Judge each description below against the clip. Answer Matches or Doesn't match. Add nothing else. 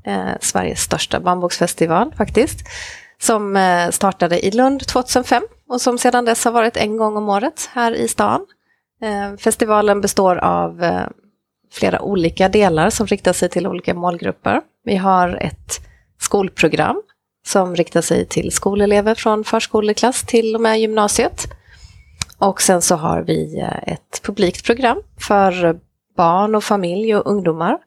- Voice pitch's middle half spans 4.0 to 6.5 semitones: Matches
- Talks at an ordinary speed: Matches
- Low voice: Doesn't match